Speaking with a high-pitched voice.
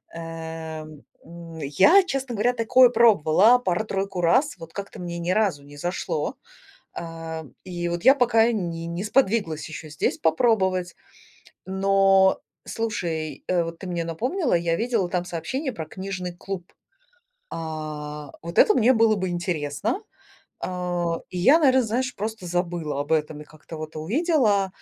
No: medium, 180 Hz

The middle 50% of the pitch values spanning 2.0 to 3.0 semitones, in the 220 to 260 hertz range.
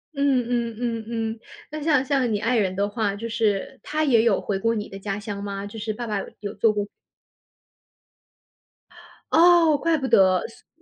No: average, 4.0 semitones; high, 225 Hz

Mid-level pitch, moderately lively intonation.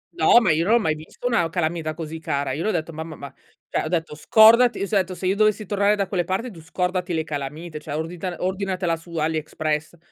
Yes: medium, 170 Hz; average, 3.6 semitones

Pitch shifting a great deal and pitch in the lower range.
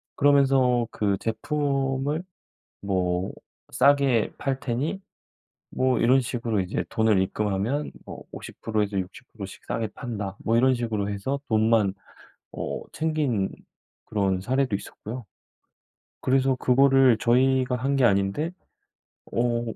No: average, 4.5 semitones; low, 120 Hz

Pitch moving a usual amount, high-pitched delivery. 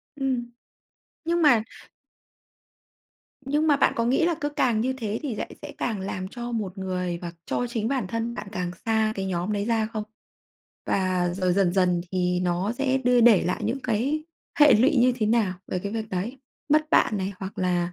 Yes: average, 5.0 semitones; high, 220 Hz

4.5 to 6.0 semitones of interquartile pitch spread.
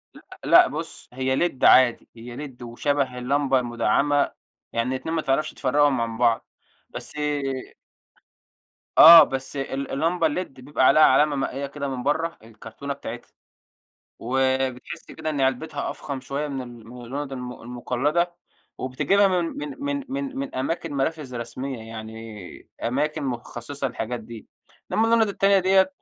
No: average, 3.7 semitones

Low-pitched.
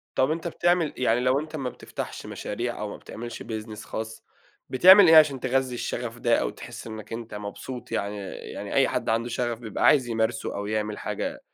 Yes: low, 120 Hz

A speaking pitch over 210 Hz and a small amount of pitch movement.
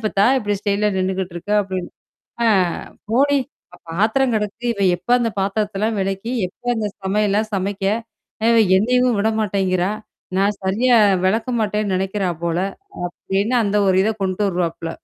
No: high, 200 Hz; narrow, 2.3 semitones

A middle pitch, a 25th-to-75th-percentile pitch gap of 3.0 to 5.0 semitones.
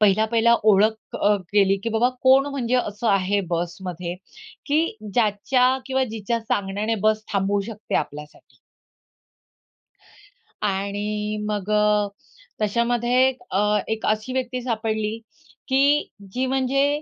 No: high, 215 Hz; average, 3.4 semitones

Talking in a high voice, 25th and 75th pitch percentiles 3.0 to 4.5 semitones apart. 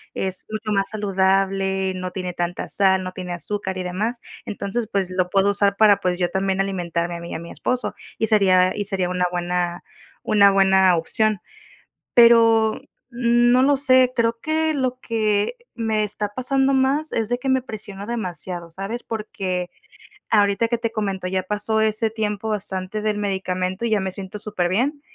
Yes: high, 200 Hz; average, 3.4 semitones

